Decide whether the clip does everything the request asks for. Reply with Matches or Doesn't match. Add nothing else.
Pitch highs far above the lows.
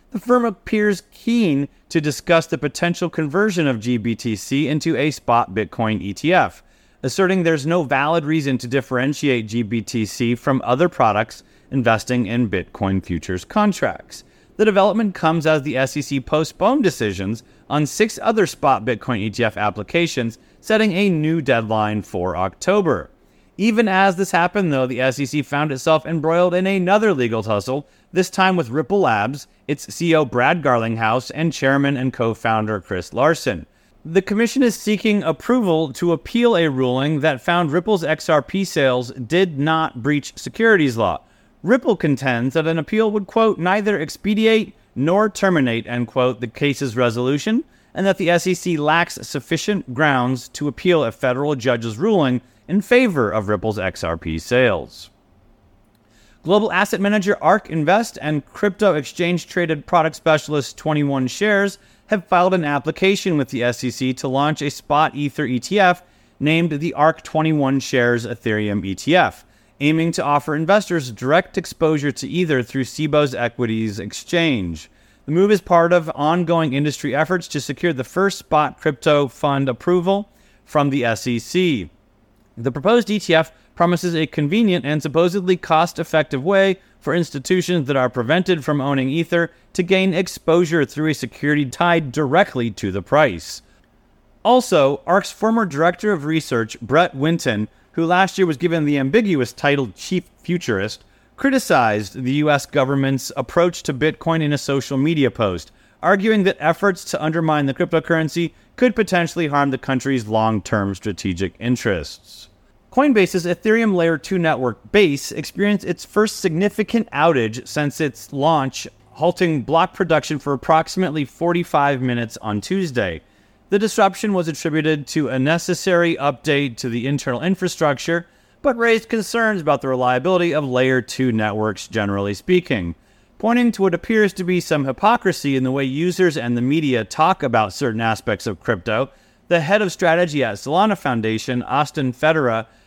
Matches